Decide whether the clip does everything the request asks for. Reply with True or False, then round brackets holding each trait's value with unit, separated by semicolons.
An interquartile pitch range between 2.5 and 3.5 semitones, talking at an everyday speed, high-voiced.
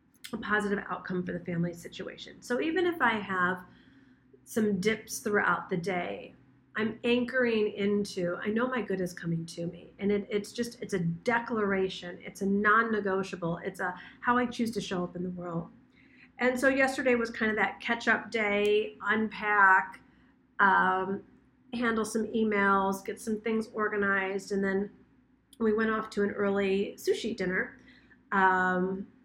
True (3.1 semitones; 160 wpm; 205 Hz)